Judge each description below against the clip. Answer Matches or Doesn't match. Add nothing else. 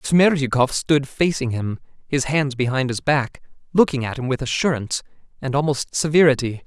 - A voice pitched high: Doesn't match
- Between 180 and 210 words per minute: Doesn't match